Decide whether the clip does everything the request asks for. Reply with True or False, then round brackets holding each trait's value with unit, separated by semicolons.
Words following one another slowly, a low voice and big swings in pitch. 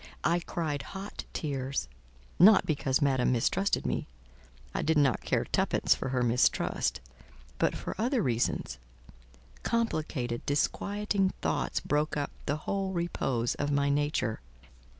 False (120 wpm; 145 Hz; 6.2 semitones)